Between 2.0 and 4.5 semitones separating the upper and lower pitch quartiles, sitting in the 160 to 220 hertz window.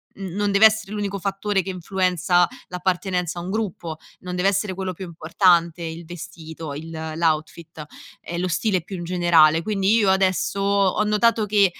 Yes: average, 2.7 semitones; medium, 185 Hz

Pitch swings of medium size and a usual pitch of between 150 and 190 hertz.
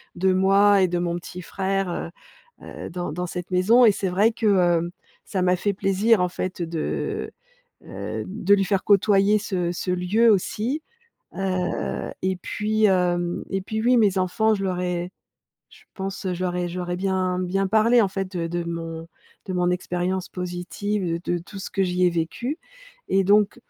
No: narrow, 2.2 semitones; medium, 185 Hz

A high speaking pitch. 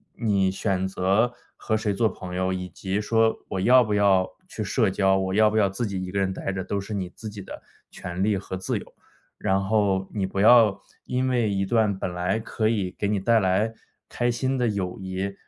No: low, 100 Hz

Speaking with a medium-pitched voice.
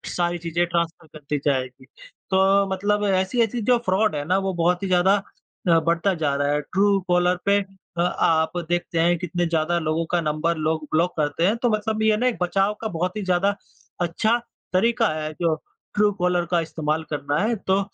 Yes: medium, 175 Hz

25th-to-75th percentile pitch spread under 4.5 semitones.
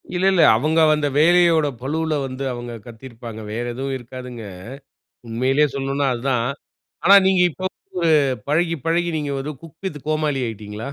No: average, 4.9 semitones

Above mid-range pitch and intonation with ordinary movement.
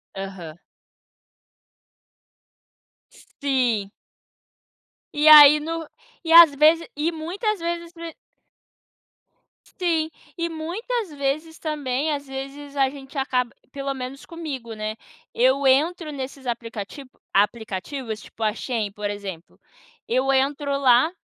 Yes: very high, 275 Hz; average, 4.6 semitones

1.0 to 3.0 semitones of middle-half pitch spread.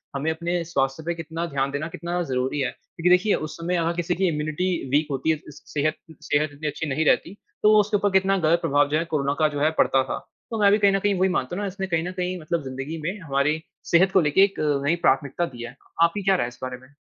No: average, 3.9 semitones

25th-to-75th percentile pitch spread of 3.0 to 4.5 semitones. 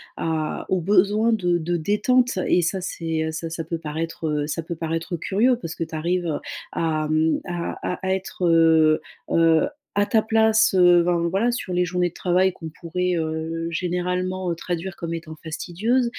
No: narrow, 2.5 semitones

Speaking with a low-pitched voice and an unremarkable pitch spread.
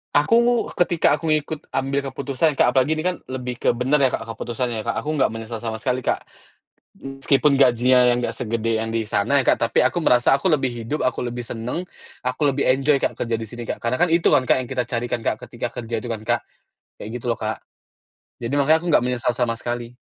Yes: low, 125 Hz; average, 3.0 semitones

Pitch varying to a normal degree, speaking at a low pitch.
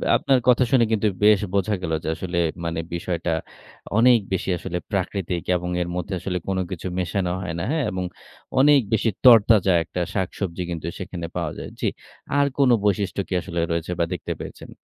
Yes: average, 3.6 semitones; very low, 95 Hz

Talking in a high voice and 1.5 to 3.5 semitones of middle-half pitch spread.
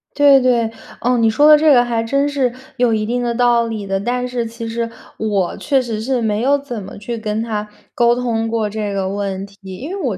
Yes: high, 230 Hz; average, 2.7 semitones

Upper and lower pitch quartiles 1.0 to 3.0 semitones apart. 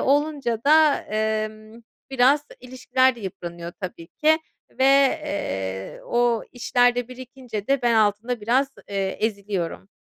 No: average, 4.2 semitones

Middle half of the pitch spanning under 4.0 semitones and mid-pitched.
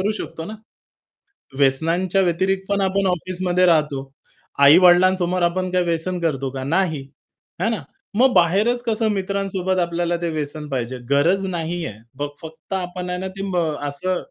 Yes: average, 2.9 semitones; medium, 180 Hz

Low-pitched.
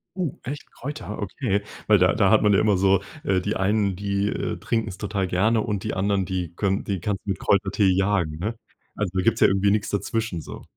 Yes: low, 100 Hz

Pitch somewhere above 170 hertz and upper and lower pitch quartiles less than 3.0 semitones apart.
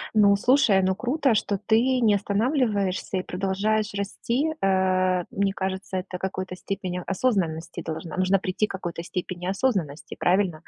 Yes: high, 190 Hz; narrow, 2.4 semitones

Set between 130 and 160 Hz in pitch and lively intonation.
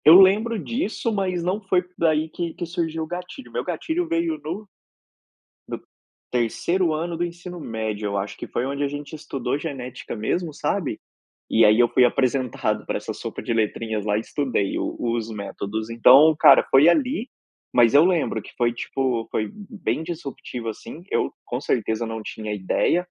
Yes: medium, 140 Hz; wide, 7.3 semitones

